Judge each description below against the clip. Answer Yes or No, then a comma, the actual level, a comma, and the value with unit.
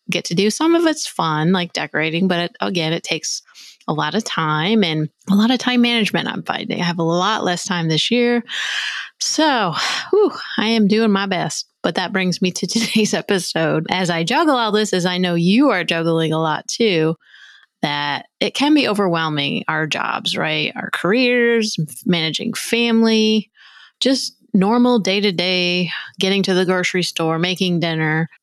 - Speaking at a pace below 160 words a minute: No, average, 180 wpm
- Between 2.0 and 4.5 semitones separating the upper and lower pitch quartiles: No, average, 5.1 semitones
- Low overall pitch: No, high, 190 Hz